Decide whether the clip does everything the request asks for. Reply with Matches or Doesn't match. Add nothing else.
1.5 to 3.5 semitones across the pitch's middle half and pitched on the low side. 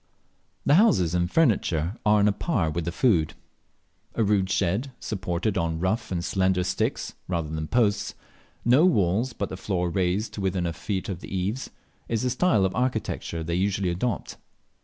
Doesn't match